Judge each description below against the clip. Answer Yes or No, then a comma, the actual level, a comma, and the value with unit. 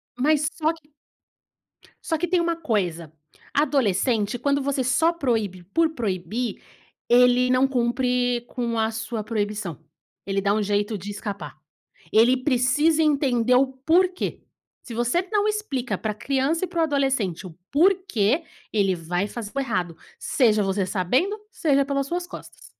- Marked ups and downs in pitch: Yes, wide, 5.9 semitones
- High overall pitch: Yes, very high, 250 Hz